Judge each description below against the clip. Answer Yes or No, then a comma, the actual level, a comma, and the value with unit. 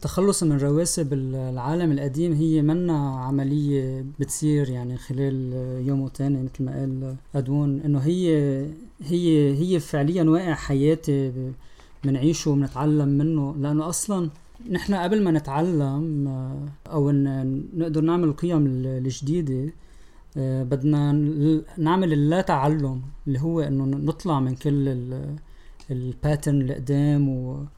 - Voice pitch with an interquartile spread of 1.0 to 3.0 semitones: Yes, average, 2.7 semitones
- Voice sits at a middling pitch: Yes, medium, 145 Hz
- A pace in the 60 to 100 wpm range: No, average, 110 wpm